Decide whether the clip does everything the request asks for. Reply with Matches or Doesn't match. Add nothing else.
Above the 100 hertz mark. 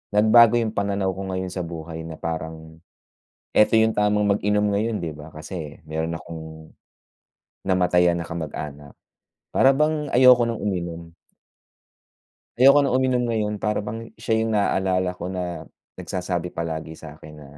Doesn't match